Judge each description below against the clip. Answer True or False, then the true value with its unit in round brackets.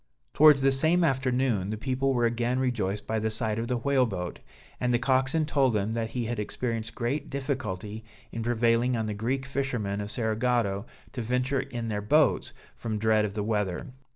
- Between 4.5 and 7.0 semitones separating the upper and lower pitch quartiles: False (3.4 semitones)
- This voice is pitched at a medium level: False (120 Hz)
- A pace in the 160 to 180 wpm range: False (190 wpm)